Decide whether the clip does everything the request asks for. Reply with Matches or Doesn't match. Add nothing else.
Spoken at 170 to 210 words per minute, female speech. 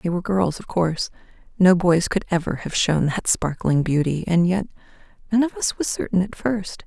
Matches